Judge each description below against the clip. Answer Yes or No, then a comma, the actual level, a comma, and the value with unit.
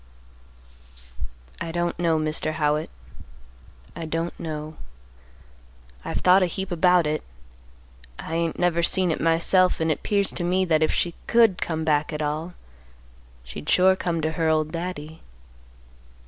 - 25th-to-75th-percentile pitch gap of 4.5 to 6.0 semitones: No, narrow, 2.4 semitones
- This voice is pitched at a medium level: Yes, medium, 165 Hz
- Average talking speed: Yes, average, 150 wpm